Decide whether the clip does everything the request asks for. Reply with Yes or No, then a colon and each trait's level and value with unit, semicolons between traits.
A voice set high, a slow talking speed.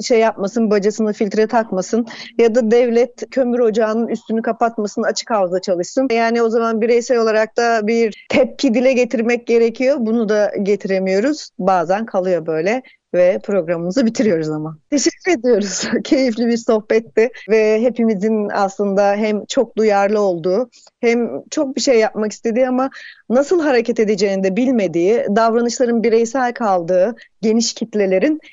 No: high, 225 Hz; average, 135 wpm